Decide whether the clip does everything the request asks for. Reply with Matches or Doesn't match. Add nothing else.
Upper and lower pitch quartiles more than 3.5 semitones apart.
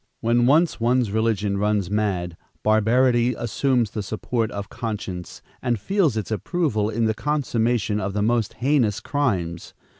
Doesn't match